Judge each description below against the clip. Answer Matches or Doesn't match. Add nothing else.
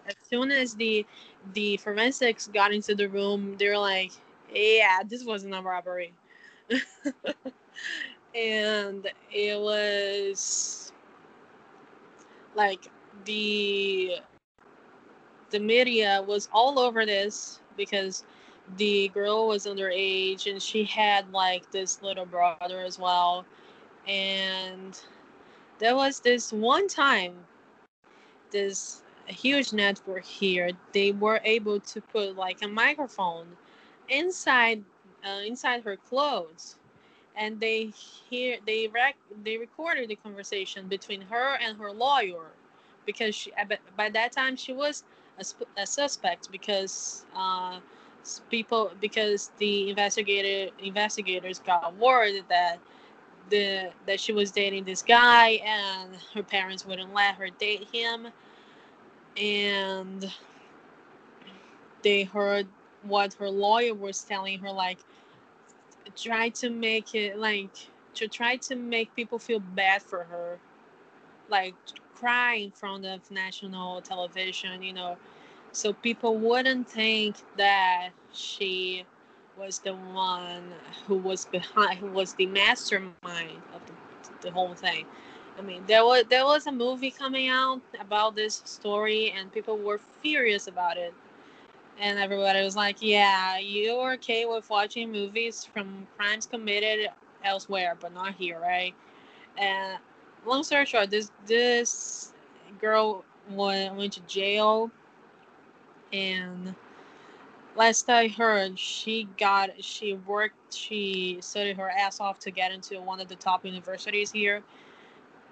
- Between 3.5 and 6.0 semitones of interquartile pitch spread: Doesn't match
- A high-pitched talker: Matches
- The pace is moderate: Doesn't match